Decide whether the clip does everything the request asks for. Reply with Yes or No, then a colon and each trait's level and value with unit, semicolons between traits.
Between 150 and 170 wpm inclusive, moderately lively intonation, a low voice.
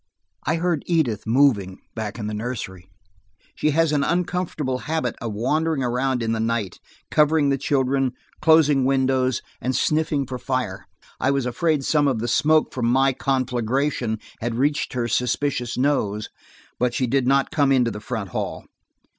Yes: average, 165 wpm; average, 3.7 semitones; low, 130 Hz